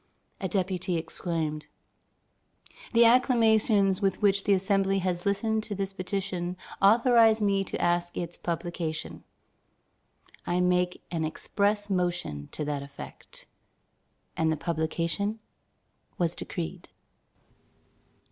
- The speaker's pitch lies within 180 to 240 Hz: Yes, medium, 185 Hz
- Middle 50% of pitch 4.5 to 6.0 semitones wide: No, average, 2.9 semitones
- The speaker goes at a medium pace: No, slow, 110 wpm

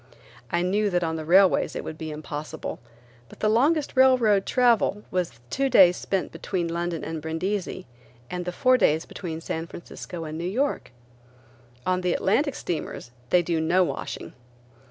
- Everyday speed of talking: Yes, average, 170 wpm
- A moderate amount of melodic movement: Yes, average, 4.2 semitones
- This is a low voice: No, medium, 180 Hz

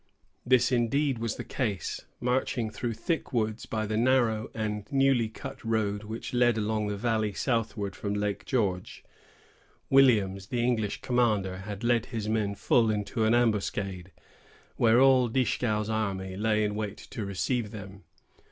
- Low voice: Yes, low, 110 Hz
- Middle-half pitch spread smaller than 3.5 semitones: Yes, average, 2.8 semitones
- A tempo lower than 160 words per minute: Yes, average, 150 wpm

